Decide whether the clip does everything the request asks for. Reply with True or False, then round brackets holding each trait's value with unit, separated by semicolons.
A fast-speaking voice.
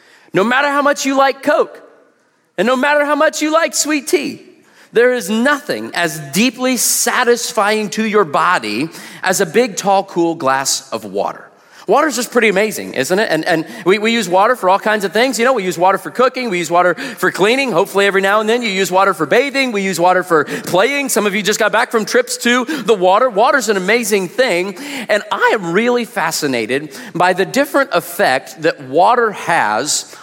True (210 wpm)